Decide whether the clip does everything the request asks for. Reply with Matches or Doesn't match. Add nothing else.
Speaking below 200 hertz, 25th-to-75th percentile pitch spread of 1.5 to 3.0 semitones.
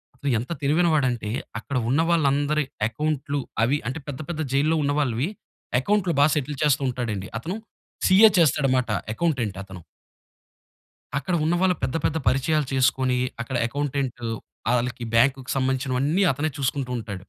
Doesn't match